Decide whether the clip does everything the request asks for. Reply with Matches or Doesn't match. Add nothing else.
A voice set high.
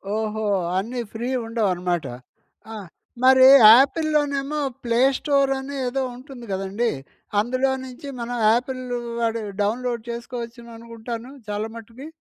Matches